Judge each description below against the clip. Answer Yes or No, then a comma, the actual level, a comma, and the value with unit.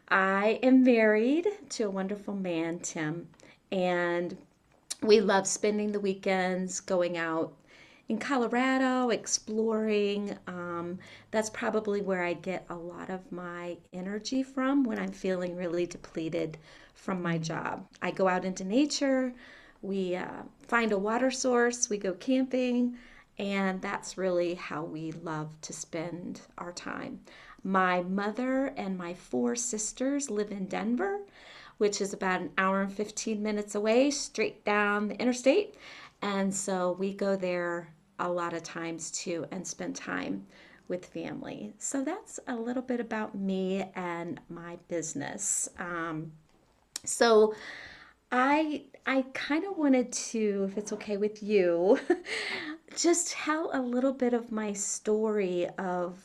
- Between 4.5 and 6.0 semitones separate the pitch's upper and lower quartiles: Yes, wide, 5.4 semitones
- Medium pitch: No, high, 205 Hz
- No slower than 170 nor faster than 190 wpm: No, average, 140 wpm